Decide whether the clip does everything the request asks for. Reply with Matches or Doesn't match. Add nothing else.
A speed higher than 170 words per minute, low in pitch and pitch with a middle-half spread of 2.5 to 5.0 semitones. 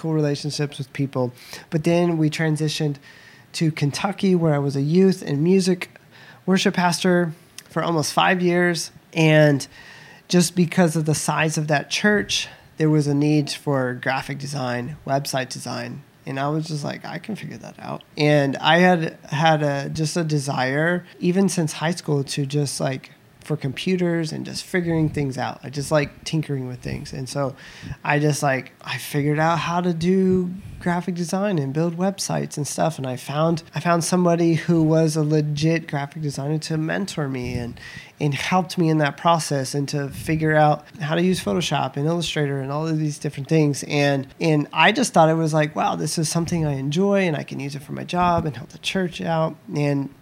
Doesn't match